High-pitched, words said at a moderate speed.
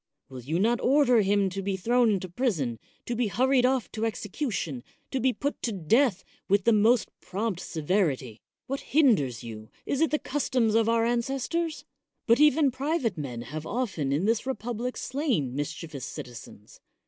Yes: high, 225 Hz; average, 170 wpm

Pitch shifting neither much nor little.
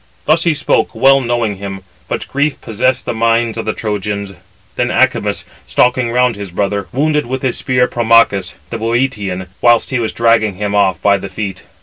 Yes: average, 3.7 semitones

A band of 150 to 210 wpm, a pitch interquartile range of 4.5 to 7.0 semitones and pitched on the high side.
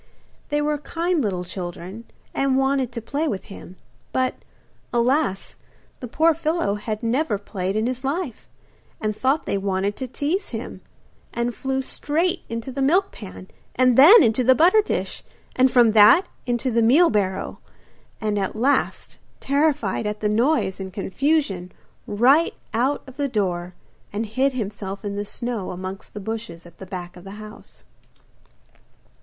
Yes: average, 160 wpm; wide, 5.6 semitones; high, 230 Hz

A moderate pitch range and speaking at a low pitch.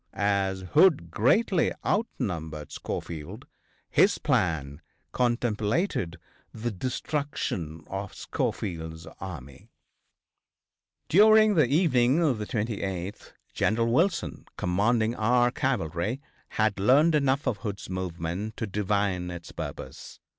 No: wide, 6.4 semitones; low, 105 Hz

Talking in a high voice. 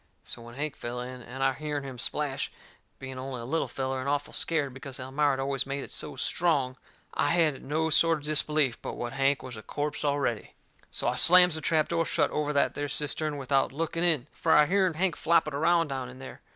No: medium, 145 Hz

